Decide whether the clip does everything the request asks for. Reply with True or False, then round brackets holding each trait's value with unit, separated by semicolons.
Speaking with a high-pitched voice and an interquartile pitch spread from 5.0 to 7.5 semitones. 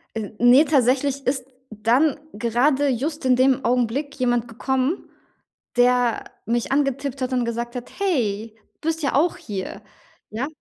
False (255 Hz; 2.8 semitones)